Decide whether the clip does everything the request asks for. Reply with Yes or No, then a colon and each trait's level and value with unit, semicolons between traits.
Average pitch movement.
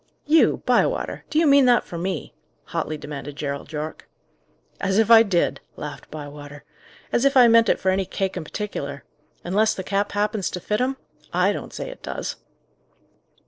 No: wide, 7.1 semitones